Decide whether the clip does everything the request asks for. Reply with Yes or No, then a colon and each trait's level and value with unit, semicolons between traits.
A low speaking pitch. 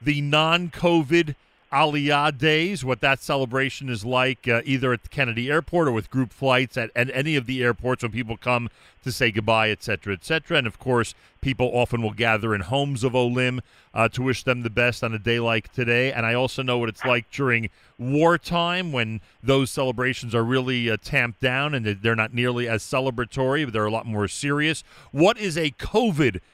Yes: low, 125 Hz